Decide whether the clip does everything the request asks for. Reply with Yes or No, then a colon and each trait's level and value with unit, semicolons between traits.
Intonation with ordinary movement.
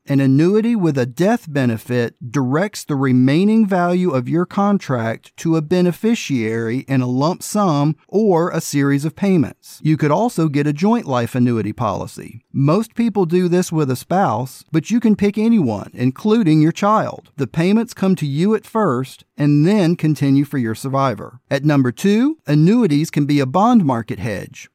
No: wide, 6.8 semitones